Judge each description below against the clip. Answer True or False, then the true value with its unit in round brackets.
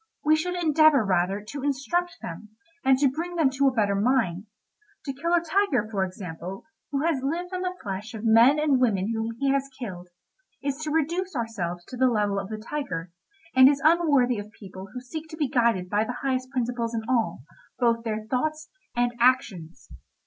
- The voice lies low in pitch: False (250 Hz)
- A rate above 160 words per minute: True (190 wpm)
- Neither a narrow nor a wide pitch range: False (5.9 semitones)